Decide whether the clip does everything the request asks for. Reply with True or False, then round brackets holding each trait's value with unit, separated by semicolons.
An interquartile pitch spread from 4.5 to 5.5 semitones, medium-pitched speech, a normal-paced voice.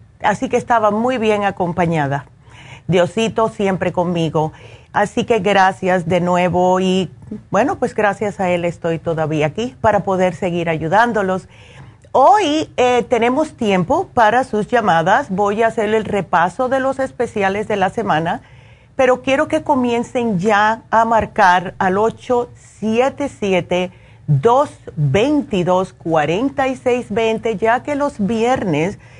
False (5.0 semitones; 205 Hz; 135 wpm)